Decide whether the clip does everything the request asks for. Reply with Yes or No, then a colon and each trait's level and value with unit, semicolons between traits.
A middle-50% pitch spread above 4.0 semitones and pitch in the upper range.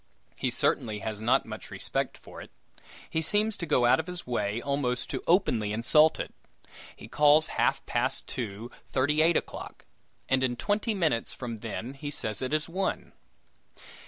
No: average, 5.3 semitones; low, 135 Hz